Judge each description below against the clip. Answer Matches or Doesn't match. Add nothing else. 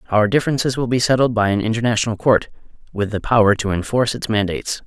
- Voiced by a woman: Doesn't match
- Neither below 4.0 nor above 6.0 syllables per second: Doesn't match